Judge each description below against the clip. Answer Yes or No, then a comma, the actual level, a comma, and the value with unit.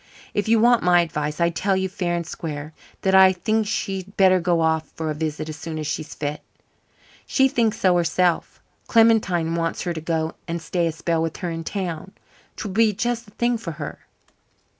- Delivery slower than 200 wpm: No, fast, 205 wpm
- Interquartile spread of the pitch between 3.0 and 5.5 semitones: Yes, average, 3.7 semitones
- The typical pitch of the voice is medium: Yes, medium, 175 Hz